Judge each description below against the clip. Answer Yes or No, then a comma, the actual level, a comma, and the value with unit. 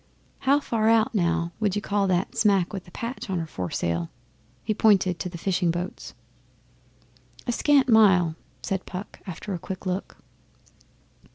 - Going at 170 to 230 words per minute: No, average, 160 wpm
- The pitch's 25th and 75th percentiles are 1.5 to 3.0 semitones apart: No, average, 3.7 semitones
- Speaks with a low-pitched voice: No, high, 190 Hz